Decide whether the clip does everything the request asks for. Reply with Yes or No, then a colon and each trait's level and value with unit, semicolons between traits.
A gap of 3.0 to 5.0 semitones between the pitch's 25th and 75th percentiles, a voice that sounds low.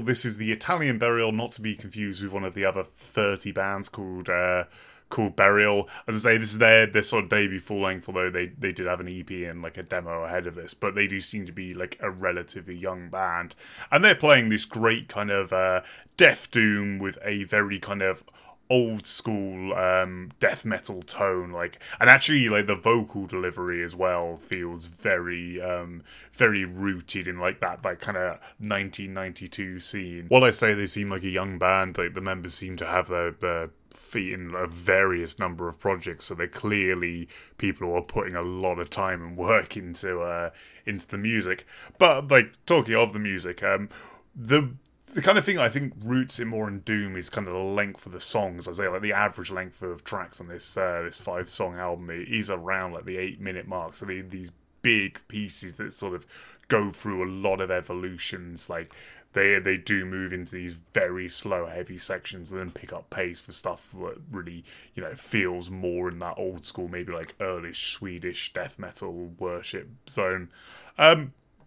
No: narrow, 2.6 semitones; very low, 95 Hz